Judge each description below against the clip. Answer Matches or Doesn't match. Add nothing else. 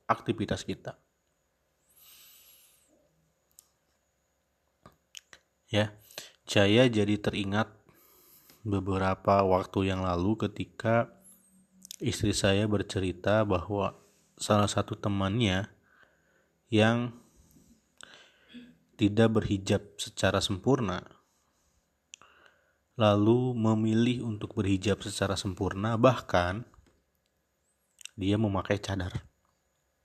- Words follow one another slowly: Matches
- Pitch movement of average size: Matches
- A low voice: Matches